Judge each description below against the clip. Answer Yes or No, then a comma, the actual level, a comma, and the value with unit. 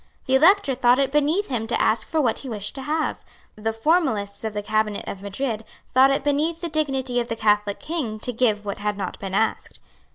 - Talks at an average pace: No, fast, 220 wpm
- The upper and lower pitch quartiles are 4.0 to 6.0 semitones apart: Yes, average, 5.1 semitones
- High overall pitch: Yes, high, 245 Hz